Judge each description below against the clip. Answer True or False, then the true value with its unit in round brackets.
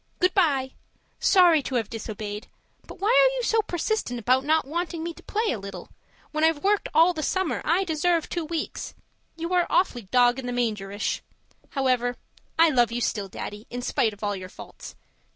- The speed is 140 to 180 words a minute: False (190 wpm)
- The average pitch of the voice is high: True (290 Hz)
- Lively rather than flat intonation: True (6.6 semitones)